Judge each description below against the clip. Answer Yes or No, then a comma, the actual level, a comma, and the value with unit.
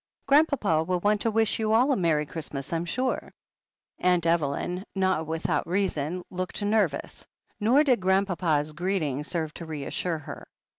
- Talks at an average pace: Yes, average, 150 wpm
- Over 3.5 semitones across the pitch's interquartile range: Yes, average, 4.6 semitones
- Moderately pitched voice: Yes, medium, 180 Hz